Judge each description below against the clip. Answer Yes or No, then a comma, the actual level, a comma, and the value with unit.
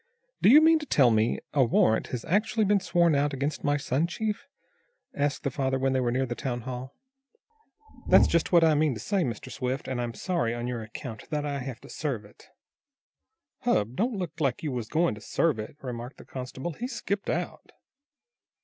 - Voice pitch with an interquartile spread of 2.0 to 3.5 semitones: No, wide, 5.4 semitones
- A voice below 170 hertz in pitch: Yes, low, 135 Hz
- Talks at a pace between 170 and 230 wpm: Yes, fast, 205 wpm